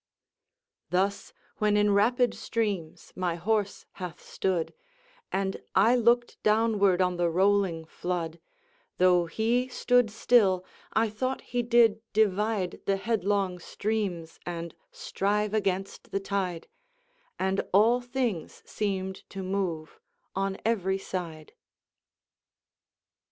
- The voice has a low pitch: No, high, 195 Hz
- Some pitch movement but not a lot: Yes, average, 3.2 semitones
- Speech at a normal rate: No, slow, 110 wpm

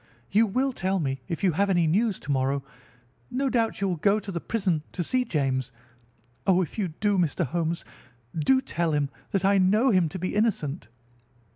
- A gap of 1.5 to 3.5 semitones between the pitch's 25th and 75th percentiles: No, average, 4.8 semitones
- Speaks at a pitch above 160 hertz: Yes, medium, 185 Hz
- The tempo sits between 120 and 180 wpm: No, average, 195 wpm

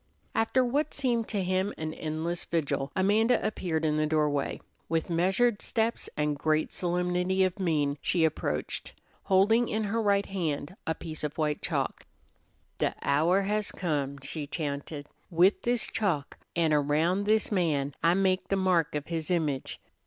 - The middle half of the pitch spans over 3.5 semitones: Yes, average, 4.5 semitones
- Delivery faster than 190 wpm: No, average, 160 wpm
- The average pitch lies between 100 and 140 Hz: No, medium, 170 Hz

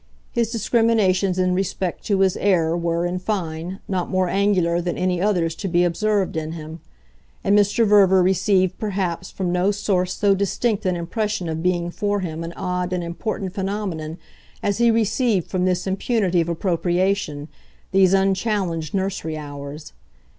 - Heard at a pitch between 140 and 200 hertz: Yes, medium, 185 Hz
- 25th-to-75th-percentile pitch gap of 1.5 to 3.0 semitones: Yes, average, 2.7 semitones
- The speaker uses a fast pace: No, average, 160 wpm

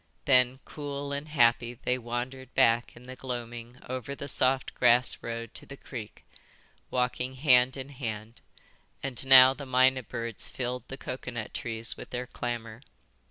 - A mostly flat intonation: Yes, narrow, 1.8 semitones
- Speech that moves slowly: No, average, 155 wpm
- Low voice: Yes, low, 125 Hz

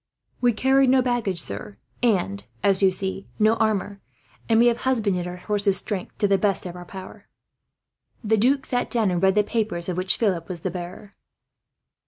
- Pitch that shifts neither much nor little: Yes, average, 3.7 semitones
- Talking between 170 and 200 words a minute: Yes, average, 190 wpm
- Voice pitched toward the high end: Yes, high, 200 Hz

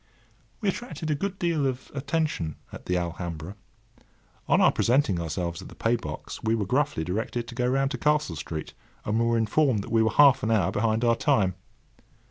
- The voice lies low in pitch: Yes, low, 115 Hz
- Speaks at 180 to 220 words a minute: Yes, average, 190 wpm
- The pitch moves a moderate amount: No, wide, 6.9 semitones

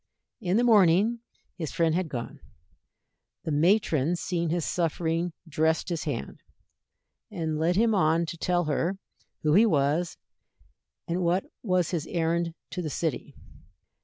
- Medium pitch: Yes, medium, 170 Hz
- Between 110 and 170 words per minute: Yes, average, 140 wpm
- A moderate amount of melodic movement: No, narrow, 2.3 semitones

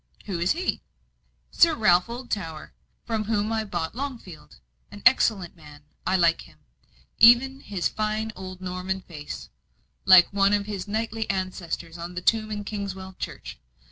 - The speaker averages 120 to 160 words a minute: Yes, average, 150 wpm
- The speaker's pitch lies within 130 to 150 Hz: No, high, 195 Hz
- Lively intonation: No, average, 3.5 semitones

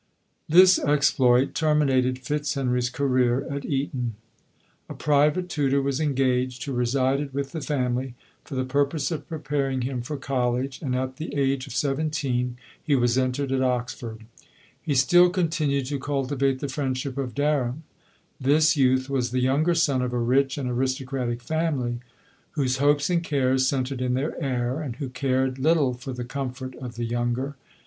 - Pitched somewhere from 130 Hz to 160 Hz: Yes, low, 135 Hz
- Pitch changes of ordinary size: No, narrow, 2.2 semitones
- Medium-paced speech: Yes, average, 170 wpm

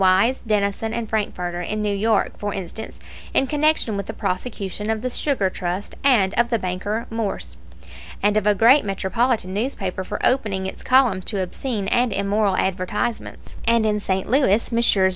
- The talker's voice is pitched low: No, high, 210 Hz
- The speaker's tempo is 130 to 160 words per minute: No, average, 170 wpm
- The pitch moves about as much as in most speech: Yes, average, 3.4 semitones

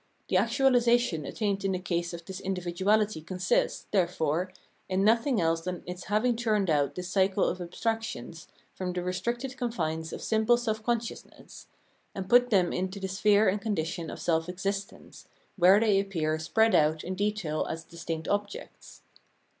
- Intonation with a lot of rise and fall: No, average, 4.0 semitones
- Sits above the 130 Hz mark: Yes, high, 190 Hz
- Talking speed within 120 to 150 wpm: No, average, 160 wpm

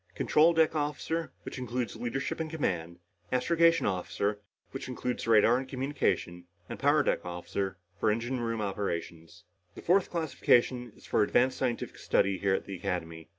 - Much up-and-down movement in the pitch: Yes, wide, 6.6 semitones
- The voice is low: Yes, low, 120 Hz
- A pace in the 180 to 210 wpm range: No, average, 155 wpm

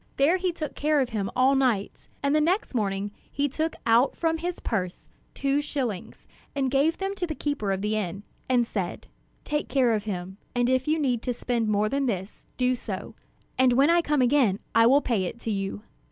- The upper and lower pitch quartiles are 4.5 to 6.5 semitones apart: Yes, wide, 5.5 semitones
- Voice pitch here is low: No, very high, 255 Hz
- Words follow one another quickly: Yes, fast, 210 wpm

